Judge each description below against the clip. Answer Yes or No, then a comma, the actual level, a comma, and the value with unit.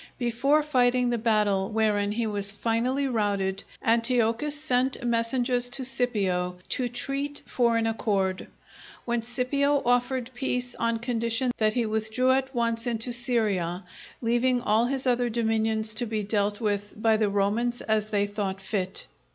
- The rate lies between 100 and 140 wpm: No, average, 150 wpm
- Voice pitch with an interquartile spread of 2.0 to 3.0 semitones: Yes, narrow, 2.6 semitones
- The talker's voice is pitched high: Yes, high, 230 Hz